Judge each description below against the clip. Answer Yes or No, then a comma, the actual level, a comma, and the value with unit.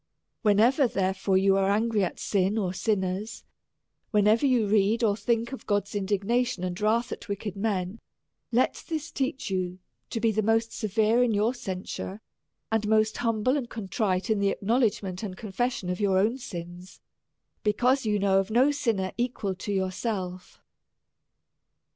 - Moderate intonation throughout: Yes, average, 3.2 semitones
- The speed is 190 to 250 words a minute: No, average, 160 wpm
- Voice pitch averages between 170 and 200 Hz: No, high, 210 Hz